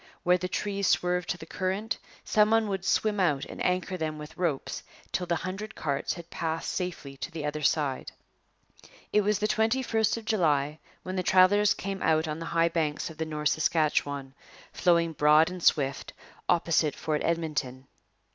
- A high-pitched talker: No, medium, 170 Hz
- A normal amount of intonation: Yes, average, 3.8 semitones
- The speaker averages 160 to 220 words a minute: Yes, average, 175 wpm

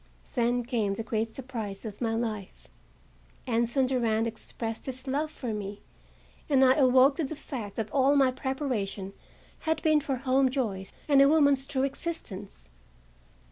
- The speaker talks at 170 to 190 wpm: No, average, 155 wpm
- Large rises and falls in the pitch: No, average, 3.7 semitones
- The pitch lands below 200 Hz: No, very high, 255 Hz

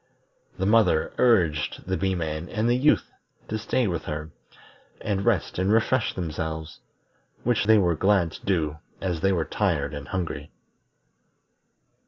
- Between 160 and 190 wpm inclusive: No, average, 150 wpm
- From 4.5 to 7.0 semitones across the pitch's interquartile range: Yes, average, 4.9 semitones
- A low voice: Yes, very low, 95 Hz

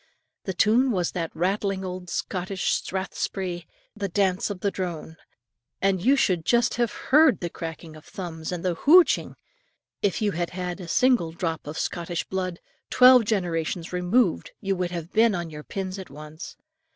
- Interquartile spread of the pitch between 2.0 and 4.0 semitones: Yes, average, 3.0 semitones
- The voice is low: No, medium, 185 Hz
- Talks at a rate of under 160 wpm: No, average, 170 wpm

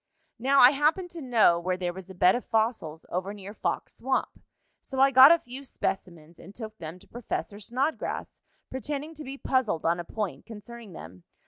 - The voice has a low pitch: No, high, 220 Hz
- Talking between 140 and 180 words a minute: No, average, 195 wpm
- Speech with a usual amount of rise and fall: No, wide, 6.6 semitones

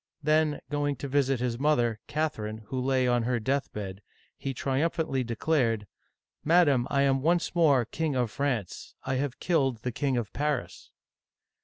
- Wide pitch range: No, average, 3.5 semitones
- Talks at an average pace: Yes, average, 165 wpm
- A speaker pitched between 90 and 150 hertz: Yes, low, 135 Hz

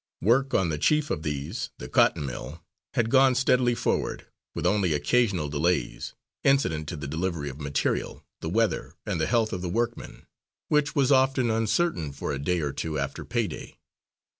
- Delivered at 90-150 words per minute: No, average, 180 wpm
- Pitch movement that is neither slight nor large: No, wide, 8.4 semitones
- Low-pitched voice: Yes, very low, 95 Hz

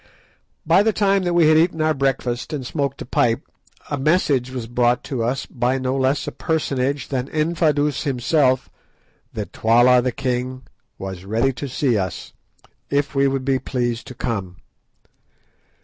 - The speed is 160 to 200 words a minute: Yes, average, 165 wpm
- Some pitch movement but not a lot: Yes, average, 3.1 semitones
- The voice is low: Yes, low, 130 Hz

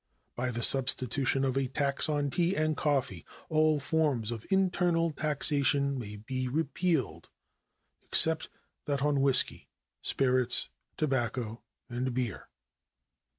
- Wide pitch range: No, average, 3.5 semitones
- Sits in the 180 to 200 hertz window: No, low, 135 Hz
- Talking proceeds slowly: Yes, slow, 115 wpm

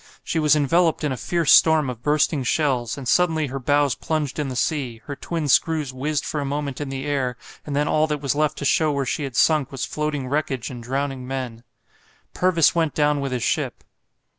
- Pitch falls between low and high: Yes, medium, 145 Hz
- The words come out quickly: Yes, fast, 215 wpm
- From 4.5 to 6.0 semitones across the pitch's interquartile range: No, narrow, 2.5 semitones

